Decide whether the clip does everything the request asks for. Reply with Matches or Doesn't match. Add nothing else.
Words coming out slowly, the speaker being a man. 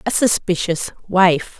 Doesn't match